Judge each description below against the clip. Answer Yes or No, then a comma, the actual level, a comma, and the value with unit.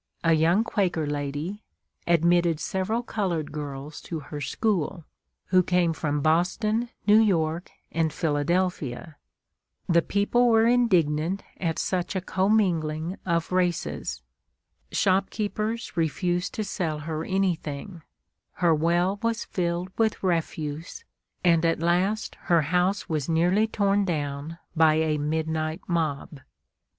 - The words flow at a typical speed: No, slow, 120 wpm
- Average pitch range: Yes, average, 3.6 semitones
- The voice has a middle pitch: Yes, medium, 170 Hz